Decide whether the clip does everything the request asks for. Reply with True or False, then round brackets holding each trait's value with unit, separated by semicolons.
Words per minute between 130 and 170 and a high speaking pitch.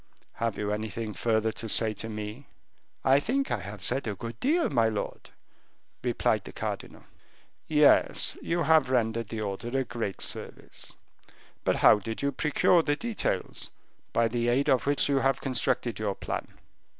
False (165 wpm; 115 Hz)